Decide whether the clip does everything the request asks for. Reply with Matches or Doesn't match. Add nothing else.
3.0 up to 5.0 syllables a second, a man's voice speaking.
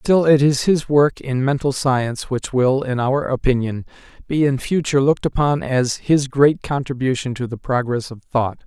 Matches